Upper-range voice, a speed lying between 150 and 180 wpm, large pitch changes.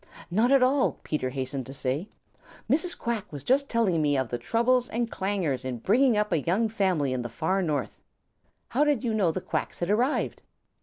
No: high, 195 Hz; average, 200 wpm; wide, 8.7 semitones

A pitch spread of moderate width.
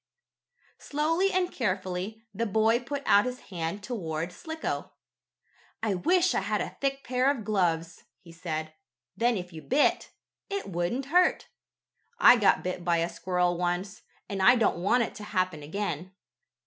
No: wide, 6.1 semitones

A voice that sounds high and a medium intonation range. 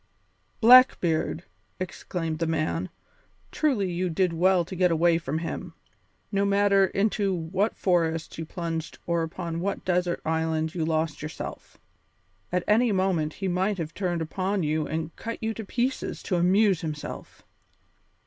No: medium, 175 Hz; average, 3.3 semitones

